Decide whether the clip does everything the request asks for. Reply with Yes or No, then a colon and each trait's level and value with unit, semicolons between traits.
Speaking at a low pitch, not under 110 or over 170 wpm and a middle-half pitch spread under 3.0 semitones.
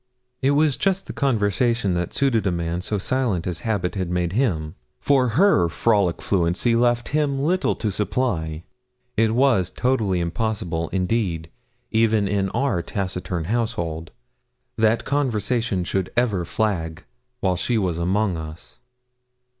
No: low, 105 Hz; average, 140 wpm; wide, 5.4 semitones